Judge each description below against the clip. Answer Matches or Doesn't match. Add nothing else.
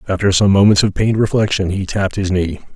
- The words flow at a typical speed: Doesn't match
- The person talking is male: Matches